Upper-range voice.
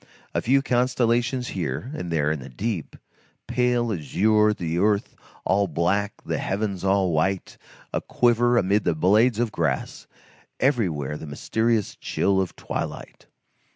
No: low, 100 Hz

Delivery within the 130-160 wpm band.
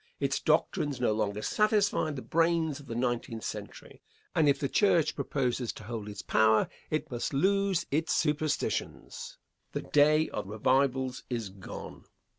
Yes: average, 150 wpm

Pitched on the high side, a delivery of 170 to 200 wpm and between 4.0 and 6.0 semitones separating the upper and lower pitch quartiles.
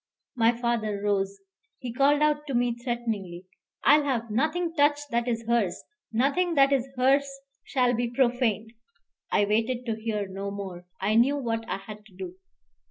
Yes: high, 235 Hz; average, 175 wpm; average, 4.3 semitones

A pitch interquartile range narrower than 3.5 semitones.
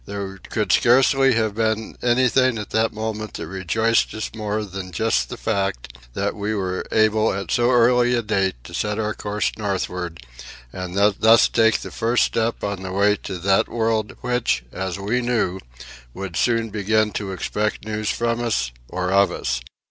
Yes: average, 2.8 semitones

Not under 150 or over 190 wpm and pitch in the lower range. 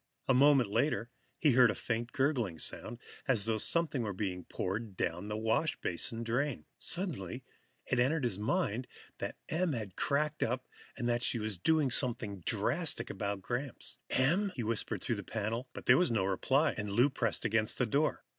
Yes: average, 180 wpm; low, 120 Hz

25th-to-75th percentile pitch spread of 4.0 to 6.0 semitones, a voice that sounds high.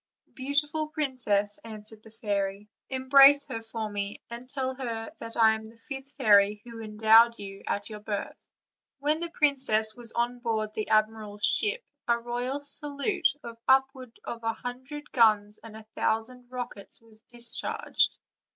No: average, 3.6 semitones; high, 230 Hz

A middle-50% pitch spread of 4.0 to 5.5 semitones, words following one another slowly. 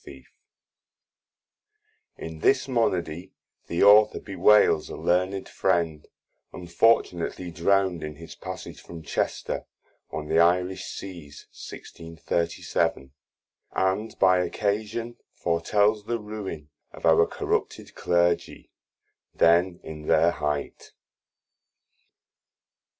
No: average, 3.5 semitones; slow, 100 wpm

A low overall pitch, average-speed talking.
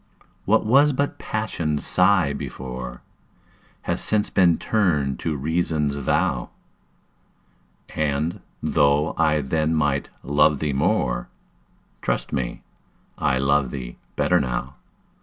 No: very low, 75 Hz; slow, 110 wpm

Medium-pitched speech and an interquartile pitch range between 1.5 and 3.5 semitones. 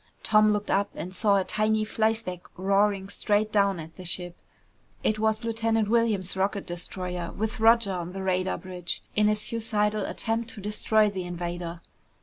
No: high, 205 Hz; average, 2.8 semitones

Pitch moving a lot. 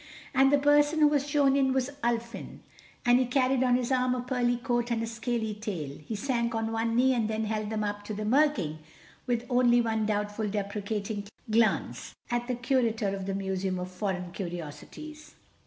No: average, 3.5 semitones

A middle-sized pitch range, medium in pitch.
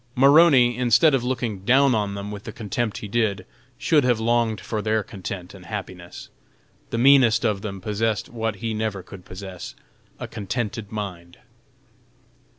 No: average, 3.3 semitones; low, 110 Hz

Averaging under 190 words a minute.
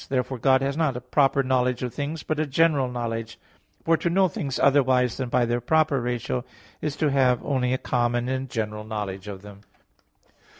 No: average, 195 wpm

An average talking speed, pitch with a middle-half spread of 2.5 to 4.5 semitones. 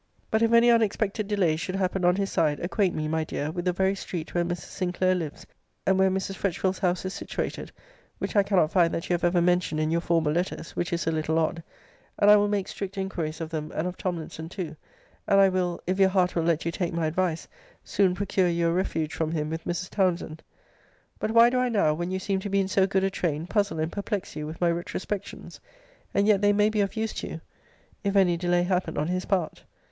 No: fast, 240 wpm; average, 2.8 semitones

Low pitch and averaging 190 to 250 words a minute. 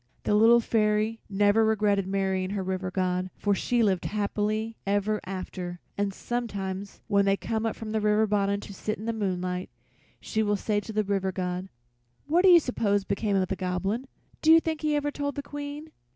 No: high, 205 Hz; average, 195 wpm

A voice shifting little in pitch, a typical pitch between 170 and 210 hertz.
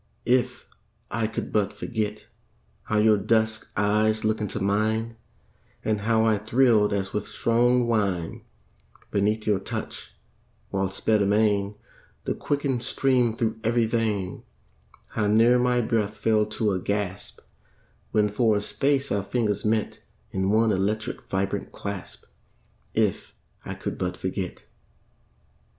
No: narrow, 2.0 semitones; low, 110 Hz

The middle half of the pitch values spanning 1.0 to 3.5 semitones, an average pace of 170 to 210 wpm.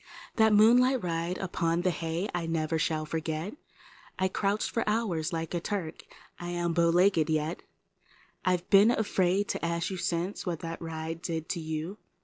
Yes: average, 2.9 semitones; average, 175 wpm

